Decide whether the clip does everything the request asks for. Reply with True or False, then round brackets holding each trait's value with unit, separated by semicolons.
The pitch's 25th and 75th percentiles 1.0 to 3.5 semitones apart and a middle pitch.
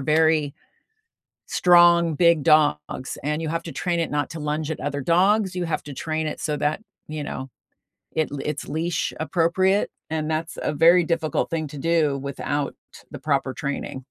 True (2.4 semitones; 155 Hz)